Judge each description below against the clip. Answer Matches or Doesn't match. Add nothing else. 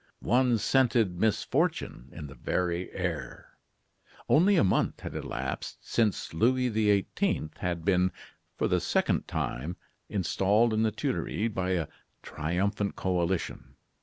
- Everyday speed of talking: Doesn't match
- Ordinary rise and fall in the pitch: Matches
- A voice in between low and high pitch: Doesn't match